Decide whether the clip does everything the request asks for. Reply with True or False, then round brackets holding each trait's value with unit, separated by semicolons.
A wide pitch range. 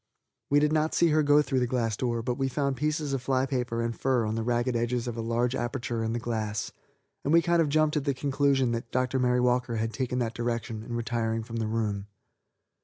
False (2.8 semitones)